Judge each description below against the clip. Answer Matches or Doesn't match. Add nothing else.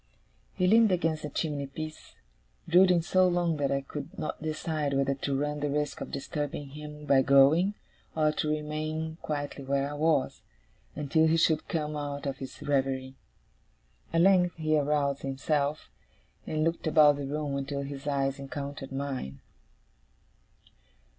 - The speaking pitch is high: Doesn't match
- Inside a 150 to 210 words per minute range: Matches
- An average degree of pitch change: Doesn't match